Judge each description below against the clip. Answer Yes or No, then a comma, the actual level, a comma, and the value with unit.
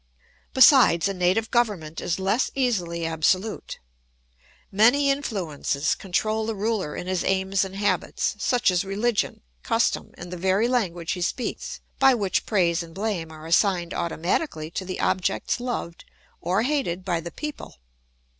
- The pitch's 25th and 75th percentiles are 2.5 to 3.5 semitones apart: No, average, 4.6 semitones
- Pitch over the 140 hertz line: Yes, high, 190 Hz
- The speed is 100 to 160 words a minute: Yes, average, 145 wpm